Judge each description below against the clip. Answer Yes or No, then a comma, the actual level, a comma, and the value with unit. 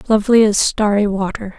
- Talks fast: No, average, 150 wpm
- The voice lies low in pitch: No, high, 210 Hz